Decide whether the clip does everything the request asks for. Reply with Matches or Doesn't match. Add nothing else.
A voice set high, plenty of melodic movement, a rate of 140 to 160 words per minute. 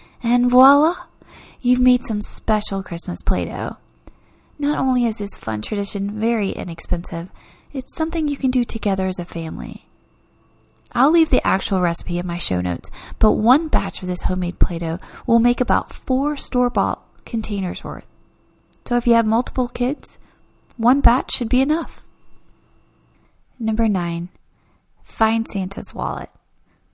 Matches